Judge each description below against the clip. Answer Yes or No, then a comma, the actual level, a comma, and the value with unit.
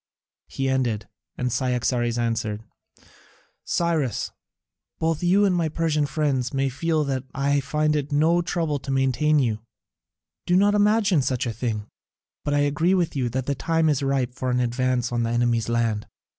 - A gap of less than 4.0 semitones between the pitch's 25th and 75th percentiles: No, average, 4.3 semitones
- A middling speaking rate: Yes, average, 175 wpm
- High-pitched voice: No, low, 135 Hz